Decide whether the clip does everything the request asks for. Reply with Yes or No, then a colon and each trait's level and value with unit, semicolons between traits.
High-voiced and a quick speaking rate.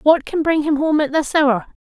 Yes: very high, 295 Hz; fast, 265 wpm